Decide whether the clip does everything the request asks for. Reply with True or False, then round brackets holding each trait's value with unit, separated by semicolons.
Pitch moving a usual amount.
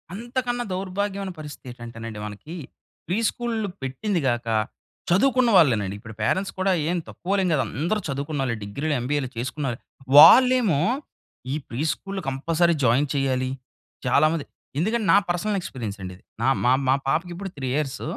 False (7.3 semitones)